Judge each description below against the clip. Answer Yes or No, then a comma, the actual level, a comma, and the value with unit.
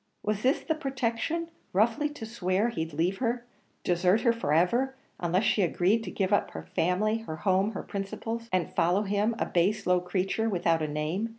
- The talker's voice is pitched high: Yes, high, 200 Hz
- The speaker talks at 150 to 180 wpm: No, average, 190 wpm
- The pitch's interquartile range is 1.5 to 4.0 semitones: No, average, 4.4 semitones